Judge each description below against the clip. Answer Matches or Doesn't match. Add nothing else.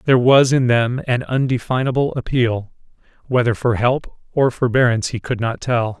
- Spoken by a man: Matches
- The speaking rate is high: Doesn't match